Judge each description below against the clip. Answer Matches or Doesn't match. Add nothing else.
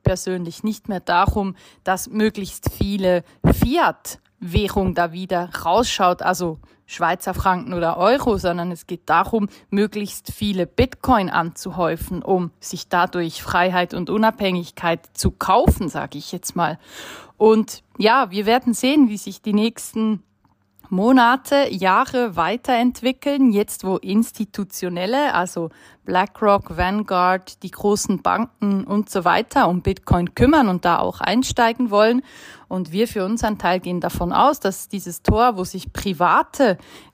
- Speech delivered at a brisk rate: Doesn't match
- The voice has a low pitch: Doesn't match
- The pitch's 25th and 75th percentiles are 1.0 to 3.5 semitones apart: Doesn't match